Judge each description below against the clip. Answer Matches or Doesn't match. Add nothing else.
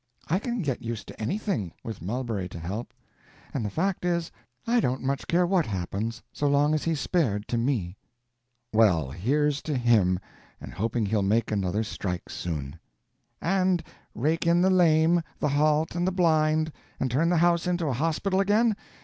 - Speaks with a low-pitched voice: Doesn't match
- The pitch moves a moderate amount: Doesn't match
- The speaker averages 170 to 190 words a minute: Matches